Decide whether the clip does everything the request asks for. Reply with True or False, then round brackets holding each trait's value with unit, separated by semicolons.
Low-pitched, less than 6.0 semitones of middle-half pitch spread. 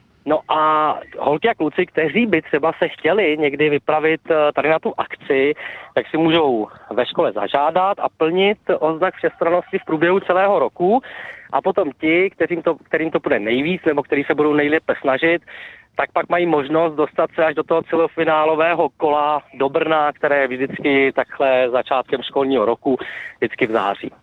False (160 Hz; 2.4 semitones)